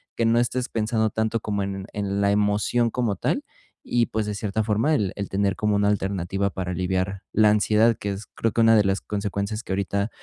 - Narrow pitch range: Yes, narrow, 1.9 semitones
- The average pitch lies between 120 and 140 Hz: No, low, 105 Hz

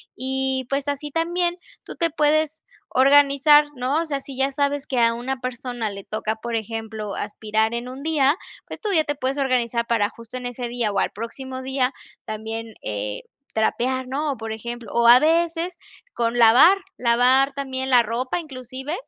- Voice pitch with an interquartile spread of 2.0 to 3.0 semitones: No, average, 3.4 semitones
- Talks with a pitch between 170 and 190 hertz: No, very high, 255 Hz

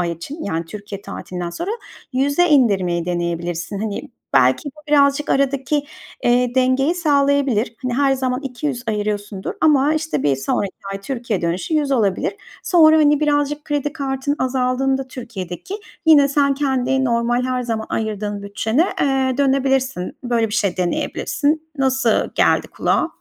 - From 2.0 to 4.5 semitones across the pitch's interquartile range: No, wide, 5.5 semitones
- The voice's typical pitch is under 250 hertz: No, very high, 255 Hz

